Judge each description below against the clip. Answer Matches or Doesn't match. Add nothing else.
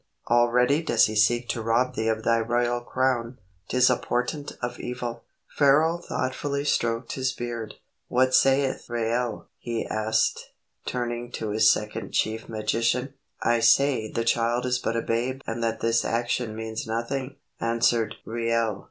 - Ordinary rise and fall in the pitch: Doesn't match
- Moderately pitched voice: Doesn't match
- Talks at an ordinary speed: Matches